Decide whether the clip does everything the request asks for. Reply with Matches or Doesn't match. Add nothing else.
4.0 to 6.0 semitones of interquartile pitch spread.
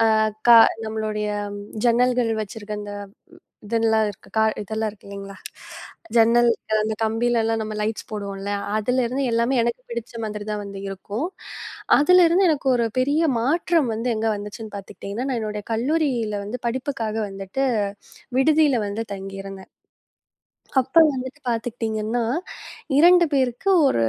Doesn't match